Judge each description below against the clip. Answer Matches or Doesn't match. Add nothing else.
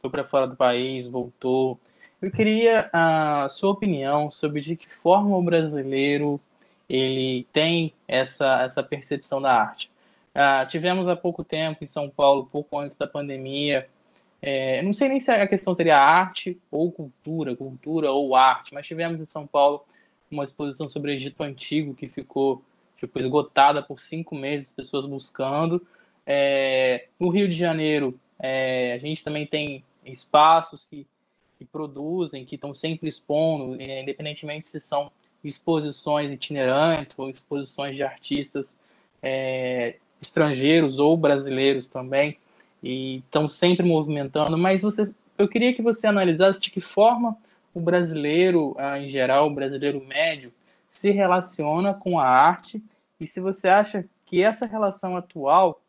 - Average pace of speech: Matches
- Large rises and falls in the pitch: Doesn't match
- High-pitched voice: Doesn't match